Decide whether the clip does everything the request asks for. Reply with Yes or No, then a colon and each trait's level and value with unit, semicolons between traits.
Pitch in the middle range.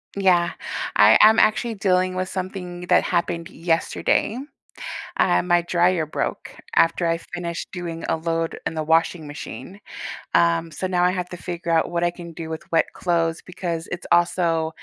Yes: medium, 175 Hz